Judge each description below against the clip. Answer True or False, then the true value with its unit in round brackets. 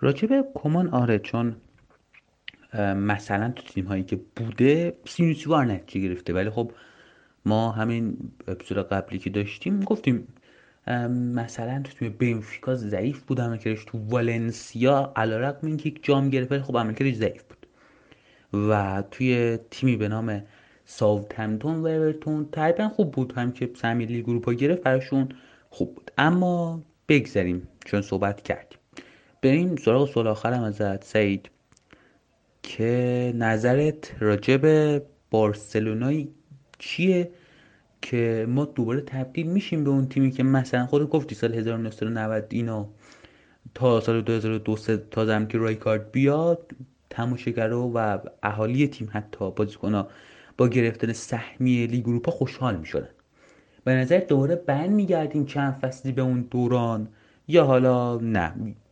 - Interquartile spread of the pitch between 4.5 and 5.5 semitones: False (4.1 semitones)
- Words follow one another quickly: False (130 wpm)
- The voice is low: True (120 Hz)